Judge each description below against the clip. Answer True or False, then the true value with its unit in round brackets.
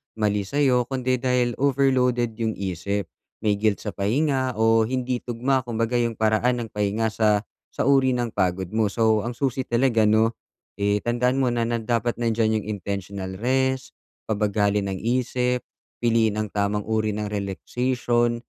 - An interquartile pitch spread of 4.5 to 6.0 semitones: False (3.1 semitones)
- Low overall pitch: True (115 Hz)